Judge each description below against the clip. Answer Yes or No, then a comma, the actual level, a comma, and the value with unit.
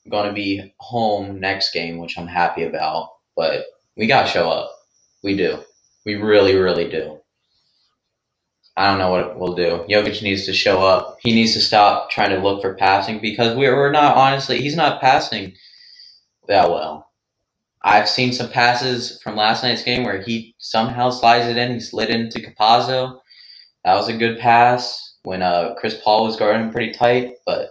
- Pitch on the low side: Yes, low, 110 Hz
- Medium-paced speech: Yes, average, 180 wpm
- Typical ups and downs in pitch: Yes, average, 3.6 semitones